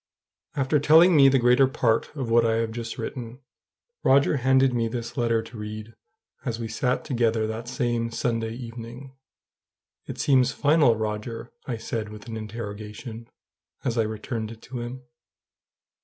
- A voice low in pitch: Yes, low, 115 Hz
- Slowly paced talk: No, average, 155 wpm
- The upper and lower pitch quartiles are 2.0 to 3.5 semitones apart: Yes, narrow, 2.4 semitones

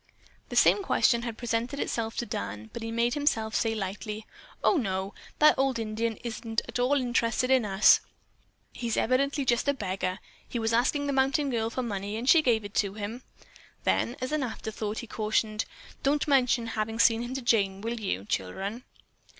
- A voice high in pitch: Yes, high, 230 Hz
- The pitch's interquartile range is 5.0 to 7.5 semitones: No, average, 3.0 semitones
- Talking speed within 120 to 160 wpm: No, average, 190 wpm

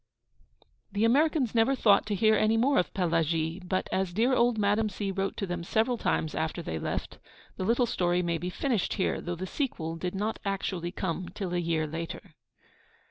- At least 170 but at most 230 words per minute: Yes, average, 190 wpm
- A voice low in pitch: No, high, 190 Hz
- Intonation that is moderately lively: Yes, average, 4.3 semitones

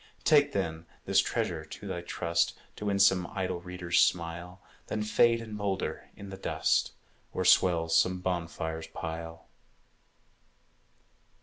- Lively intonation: No, average, 2.9 semitones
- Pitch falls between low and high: No, very low, 90 Hz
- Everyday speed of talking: No, slow, 130 wpm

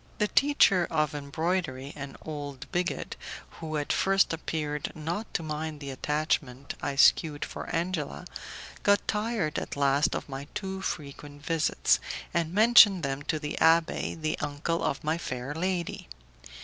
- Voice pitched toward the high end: No, medium, 155 Hz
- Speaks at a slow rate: No, average, 150 wpm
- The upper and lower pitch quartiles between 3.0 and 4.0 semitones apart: Yes, average, 3.4 semitones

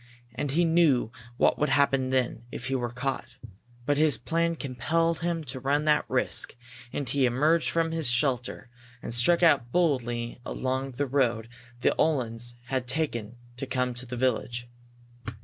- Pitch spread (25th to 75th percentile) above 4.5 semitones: No, average, 4.0 semitones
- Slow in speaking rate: No, average, 165 wpm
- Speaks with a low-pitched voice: Yes, low, 130 Hz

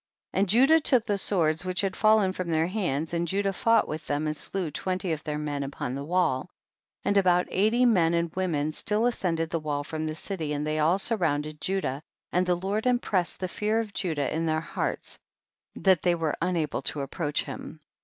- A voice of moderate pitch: Yes, medium, 175 Hz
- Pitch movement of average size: Yes, average, 4.1 semitones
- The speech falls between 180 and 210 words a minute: Yes, fast, 205 wpm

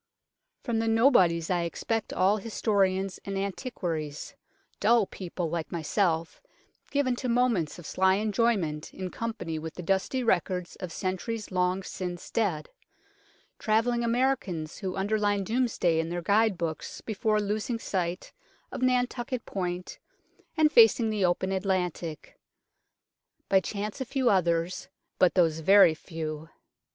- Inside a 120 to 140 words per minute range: Yes, slow, 135 wpm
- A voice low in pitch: No, high, 190 Hz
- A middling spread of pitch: Yes, average, 4.5 semitones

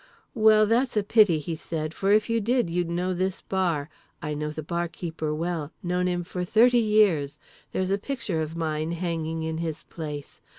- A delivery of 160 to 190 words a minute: Yes, average, 185 wpm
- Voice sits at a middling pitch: Yes, medium, 175 Hz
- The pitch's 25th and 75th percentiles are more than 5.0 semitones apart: No, average, 4.2 semitones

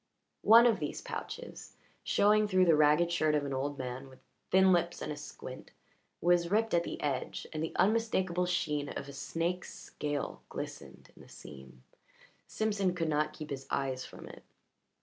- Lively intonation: No, average, 4.2 semitones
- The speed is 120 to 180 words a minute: Yes, average, 175 wpm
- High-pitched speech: No, medium, 160 Hz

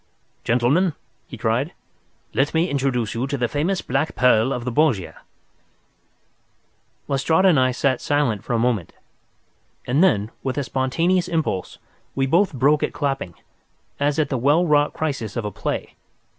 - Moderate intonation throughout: Yes, average, 3.9 semitones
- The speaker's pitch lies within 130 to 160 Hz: Yes, low, 135 Hz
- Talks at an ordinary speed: Yes, average, 155 wpm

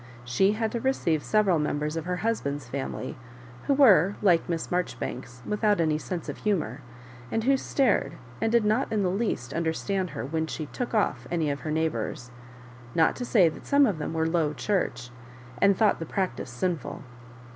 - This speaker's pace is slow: No, average, 185 wpm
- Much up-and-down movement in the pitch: Yes, wide, 5.8 semitones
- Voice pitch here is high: No, medium, 170 Hz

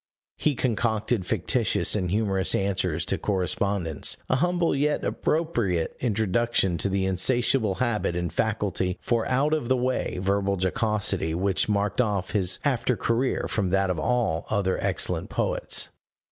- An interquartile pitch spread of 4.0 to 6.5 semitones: Yes, average, 4.4 semitones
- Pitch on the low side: Yes, low, 105 Hz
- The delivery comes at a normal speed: Yes, average, 145 wpm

